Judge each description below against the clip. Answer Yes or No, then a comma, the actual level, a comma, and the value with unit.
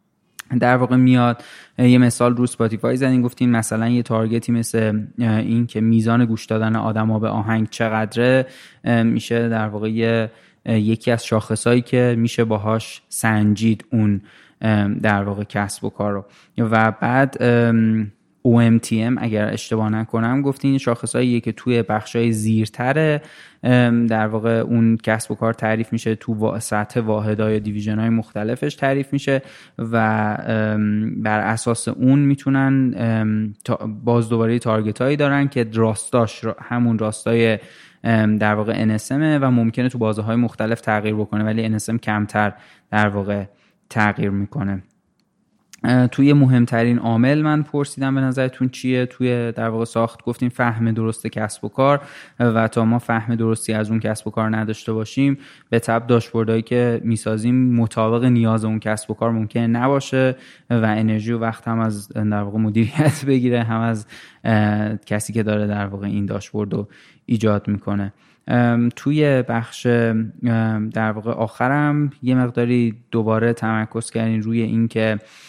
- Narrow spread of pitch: Yes, narrow, 1.9 semitones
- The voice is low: Yes, low, 115 Hz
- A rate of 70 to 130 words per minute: No, average, 140 wpm